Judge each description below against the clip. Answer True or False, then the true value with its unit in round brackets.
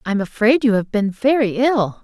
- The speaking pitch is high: True (230 Hz)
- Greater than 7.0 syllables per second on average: False (5.2 syllables/s)